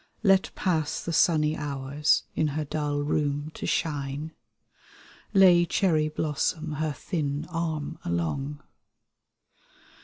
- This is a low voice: No, medium, 150 Hz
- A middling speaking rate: No, slow, 110 wpm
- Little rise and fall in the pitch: Yes, narrow, 1.9 semitones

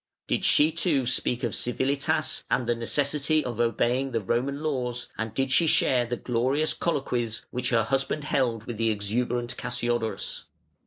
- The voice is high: No, low, 125 Hz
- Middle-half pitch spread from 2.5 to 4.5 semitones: Yes, average, 2.8 semitones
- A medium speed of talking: Yes, average, 160 wpm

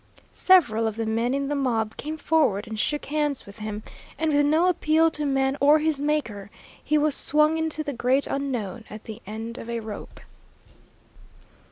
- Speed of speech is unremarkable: Yes, average, 185 wpm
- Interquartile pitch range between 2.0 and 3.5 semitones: No, average, 5.3 semitones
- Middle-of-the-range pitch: No, very high, 275 Hz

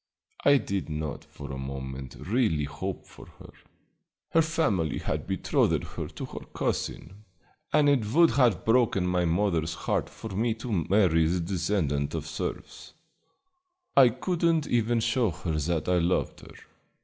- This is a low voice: Yes, very low, 95 Hz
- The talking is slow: No, average, 155 wpm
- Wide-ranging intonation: Yes, wide, 7.0 semitones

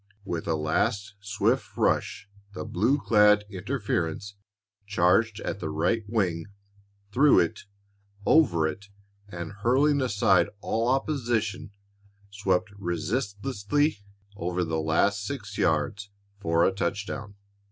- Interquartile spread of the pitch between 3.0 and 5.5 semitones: Yes, average, 4.6 semitones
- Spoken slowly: Yes, slow, 110 wpm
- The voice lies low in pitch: Yes, low, 100 Hz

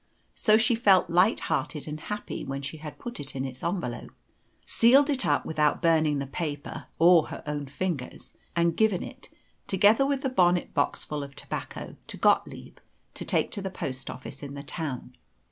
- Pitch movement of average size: No, wide, 6.0 semitones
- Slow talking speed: No, average, 180 wpm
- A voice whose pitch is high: No, medium, 165 Hz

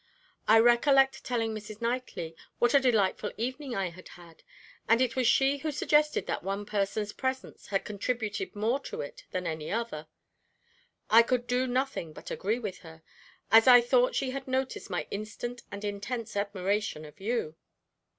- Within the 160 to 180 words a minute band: Yes, average, 170 wpm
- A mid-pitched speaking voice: No, high, 225 Hz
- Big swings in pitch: No, average, 4.1 semitones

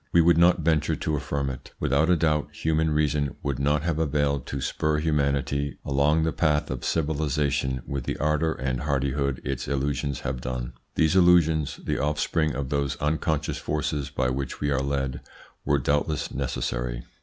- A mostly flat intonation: Yes, narrow, 2.2 semitones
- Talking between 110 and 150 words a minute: No, average, 170 wpm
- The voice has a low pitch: Yes, very low, 70 Hz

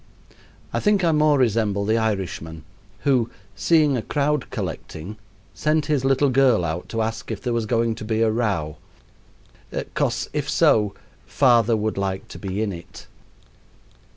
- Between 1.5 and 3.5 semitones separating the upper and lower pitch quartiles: No, average, 4.9 semitones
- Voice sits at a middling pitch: No, low, 115 Hz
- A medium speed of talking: Yes, average, 155 wpm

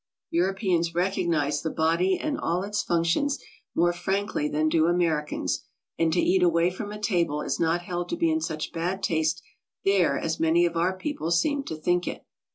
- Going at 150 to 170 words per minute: No, average, 190 wpm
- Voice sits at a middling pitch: Yes, medium, 175 Hz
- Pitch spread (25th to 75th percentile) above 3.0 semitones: No, average, 2.7 semitones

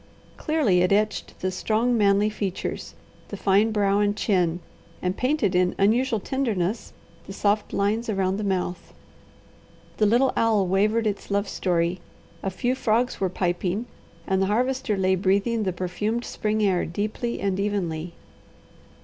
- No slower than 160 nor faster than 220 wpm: No, average, 150 wpm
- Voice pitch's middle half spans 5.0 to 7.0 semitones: No, average, 2.9 semitones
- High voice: Yes, high, 200 Hz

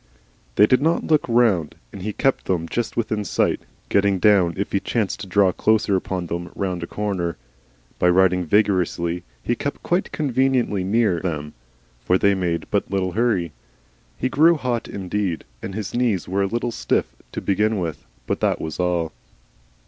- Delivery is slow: No, average, 175 wpm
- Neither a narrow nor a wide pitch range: Yes, average, 4.4 semitones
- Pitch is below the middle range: Yes, low, 100 Hz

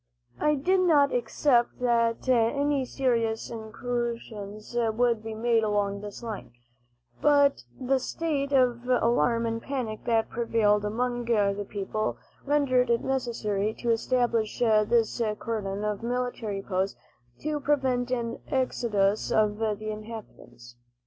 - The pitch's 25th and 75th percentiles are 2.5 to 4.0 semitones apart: Yes, average, 2.8 semitones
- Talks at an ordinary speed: No, slow, 120 wpm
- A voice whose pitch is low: No, high, 230 Hz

